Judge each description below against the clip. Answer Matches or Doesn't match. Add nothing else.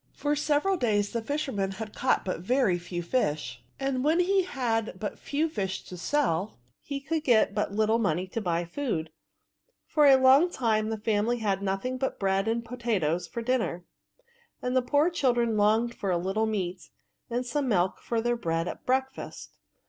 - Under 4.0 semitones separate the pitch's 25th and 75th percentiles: Doesn't match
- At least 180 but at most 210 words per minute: Matches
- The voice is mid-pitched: Doesn't match